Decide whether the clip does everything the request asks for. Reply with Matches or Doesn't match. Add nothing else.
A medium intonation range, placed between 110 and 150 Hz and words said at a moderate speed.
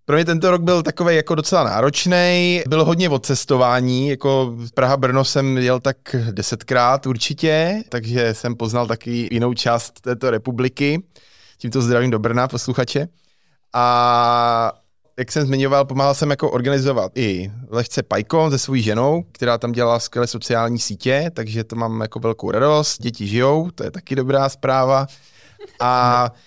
Matches